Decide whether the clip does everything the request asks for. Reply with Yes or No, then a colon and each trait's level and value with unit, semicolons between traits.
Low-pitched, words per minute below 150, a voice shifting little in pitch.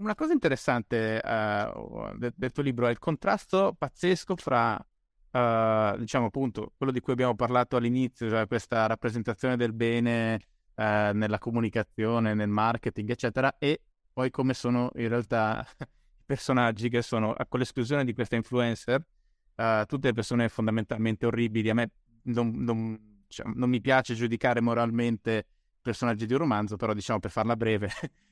No: low, 120 Hz; average, 155 wpm; narrow, 2.0 semitones